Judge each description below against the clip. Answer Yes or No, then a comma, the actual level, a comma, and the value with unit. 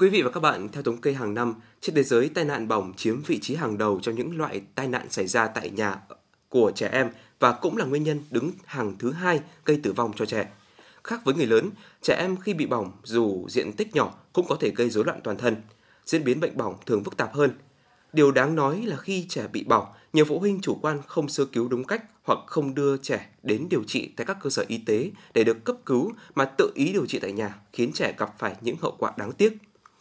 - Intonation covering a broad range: Yes, wide, 7.1 semitones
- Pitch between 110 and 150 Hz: Yes, medium, 140 Hz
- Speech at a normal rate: No, fast, 255 wpm